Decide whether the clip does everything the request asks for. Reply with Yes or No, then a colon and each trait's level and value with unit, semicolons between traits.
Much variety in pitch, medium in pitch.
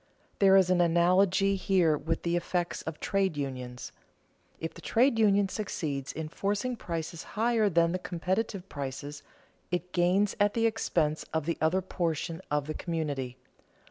No: average, 3.8 semitones; medium, 175 Hz